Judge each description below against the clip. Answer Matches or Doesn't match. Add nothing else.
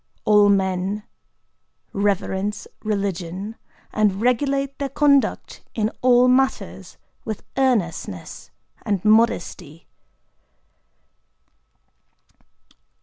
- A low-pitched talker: Doesn't match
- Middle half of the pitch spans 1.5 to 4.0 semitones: Doesn't match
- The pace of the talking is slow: Matches